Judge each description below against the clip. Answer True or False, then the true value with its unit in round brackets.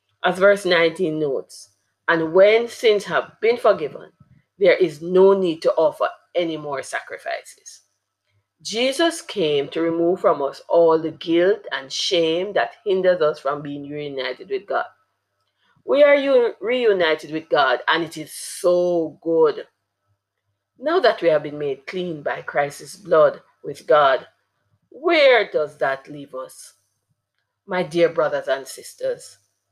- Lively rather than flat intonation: True (7.6 semitones)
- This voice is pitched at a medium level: True (170 Hz)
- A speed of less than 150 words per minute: True (140 wpm)